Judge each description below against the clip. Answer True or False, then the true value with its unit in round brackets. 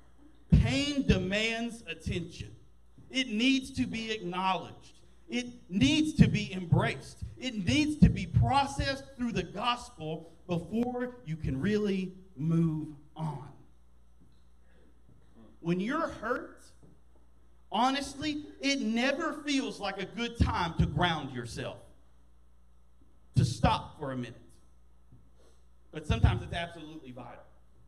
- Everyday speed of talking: False (110 wpm)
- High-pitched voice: False (175 Hz)